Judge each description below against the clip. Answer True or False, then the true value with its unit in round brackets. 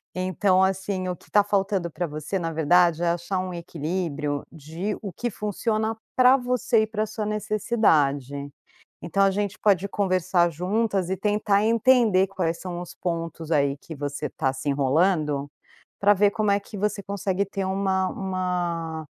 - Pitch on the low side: False (185 Hz)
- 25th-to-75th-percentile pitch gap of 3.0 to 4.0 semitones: True (3.6 semitones)